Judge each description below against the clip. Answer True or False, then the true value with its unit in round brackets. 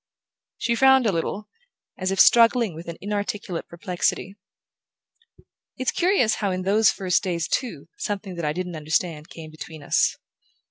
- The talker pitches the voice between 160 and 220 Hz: True (190 Hz)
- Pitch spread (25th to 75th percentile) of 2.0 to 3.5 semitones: False (4.2 semitones)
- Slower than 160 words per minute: True (150 wpm)